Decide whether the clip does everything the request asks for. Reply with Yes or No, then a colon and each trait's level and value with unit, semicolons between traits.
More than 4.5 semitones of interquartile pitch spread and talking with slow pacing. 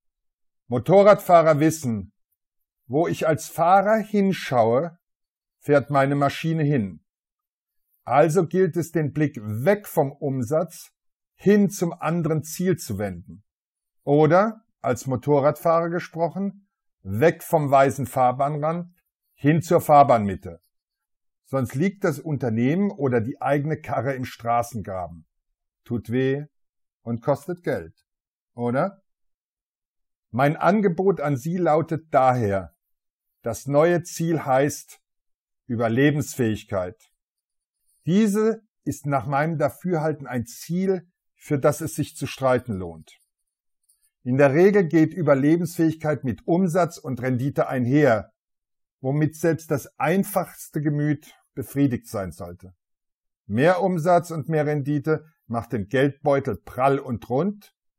Yes: average, 5.2 semitones; slow, 110 wpm